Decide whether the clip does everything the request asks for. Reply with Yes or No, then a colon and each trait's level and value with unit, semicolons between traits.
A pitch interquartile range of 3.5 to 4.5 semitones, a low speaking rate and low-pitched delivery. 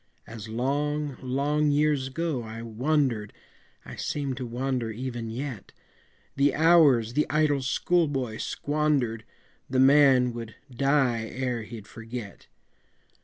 Yes: average, 4.0 semitones; slow, 120 wpm; low, 130 Hz